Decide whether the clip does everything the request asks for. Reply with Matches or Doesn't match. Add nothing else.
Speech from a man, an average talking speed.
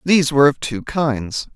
Matches